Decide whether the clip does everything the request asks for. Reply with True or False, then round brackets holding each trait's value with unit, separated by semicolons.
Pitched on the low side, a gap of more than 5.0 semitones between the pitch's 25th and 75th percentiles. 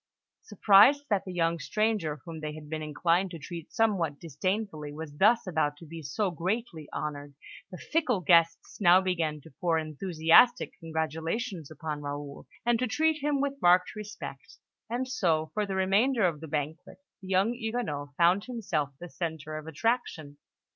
False (170 Hz; 5.5 semitones)